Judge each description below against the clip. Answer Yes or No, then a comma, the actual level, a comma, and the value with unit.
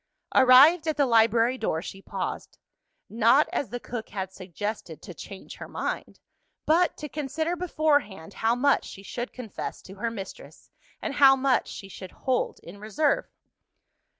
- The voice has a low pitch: No, high, 240 Hz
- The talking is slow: No, average, 155 wpm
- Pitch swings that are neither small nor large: No, wide, 6.1 semitones